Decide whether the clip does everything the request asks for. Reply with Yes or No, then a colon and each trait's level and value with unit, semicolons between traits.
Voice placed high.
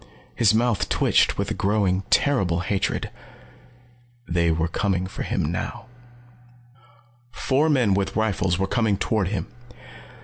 No: low, 100 Hz